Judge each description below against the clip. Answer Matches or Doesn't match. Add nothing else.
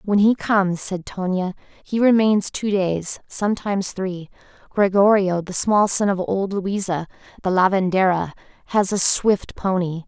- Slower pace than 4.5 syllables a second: Matches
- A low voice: Doesn't match